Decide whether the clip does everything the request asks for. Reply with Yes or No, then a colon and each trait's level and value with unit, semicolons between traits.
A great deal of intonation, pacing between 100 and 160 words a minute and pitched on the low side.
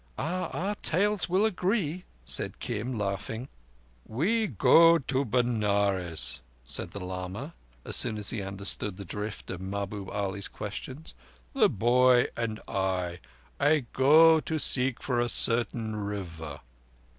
Yes: wide, 6.7 semitones; slow, 135 wpm; low, 115 Hz